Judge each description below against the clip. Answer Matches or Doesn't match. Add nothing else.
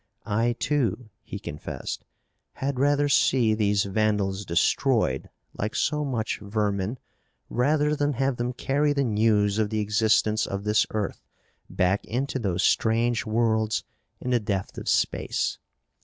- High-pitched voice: Doesn't match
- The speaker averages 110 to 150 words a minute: Matches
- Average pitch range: Matches